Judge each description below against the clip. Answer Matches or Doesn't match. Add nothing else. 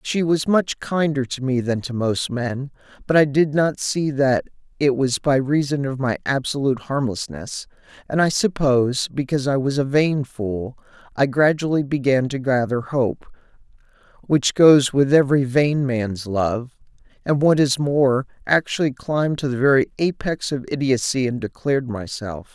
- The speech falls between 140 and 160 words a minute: Matches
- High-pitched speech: Doesn't match